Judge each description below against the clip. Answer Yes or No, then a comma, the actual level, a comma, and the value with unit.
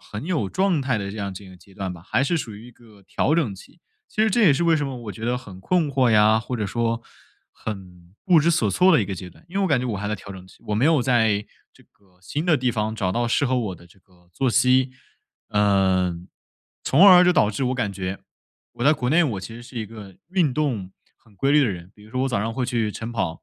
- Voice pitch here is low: Yes, low, 115 Hz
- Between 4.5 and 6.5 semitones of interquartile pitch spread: Yes, wide, 5.6 semitones